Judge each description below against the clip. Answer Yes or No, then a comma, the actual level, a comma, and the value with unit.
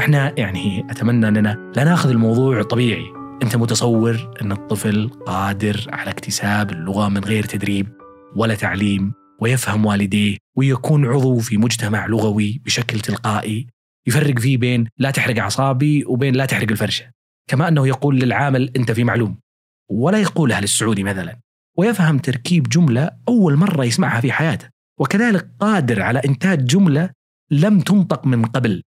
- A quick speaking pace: Yes, fast, 140 wpm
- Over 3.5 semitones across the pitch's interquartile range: Yes, average, 4.9 semitones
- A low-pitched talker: Yes, low, 120 Hz